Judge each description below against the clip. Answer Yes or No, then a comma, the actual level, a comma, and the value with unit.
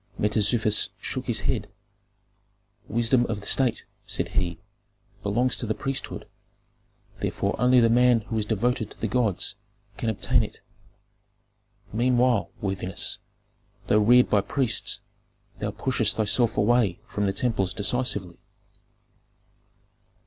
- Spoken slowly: Yes, slow, 120 wpm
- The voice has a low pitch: Yes, low, 110 Hz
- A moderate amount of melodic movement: Yes, average, 3.2 semitones